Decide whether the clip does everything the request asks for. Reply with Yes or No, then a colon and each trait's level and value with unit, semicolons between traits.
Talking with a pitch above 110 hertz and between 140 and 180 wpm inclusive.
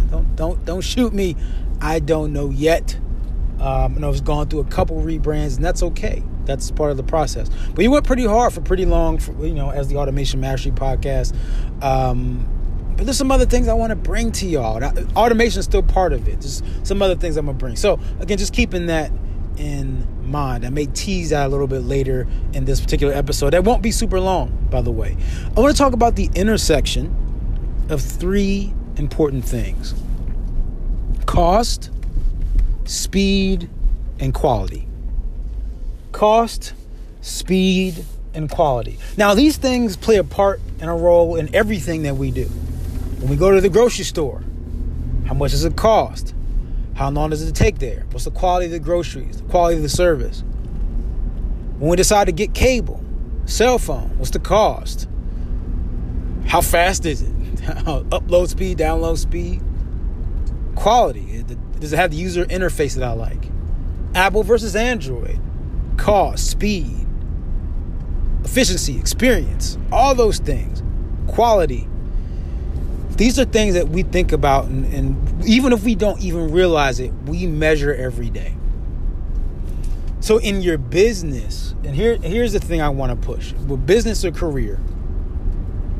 Yes: low, 135 Hz; average, 165 wpm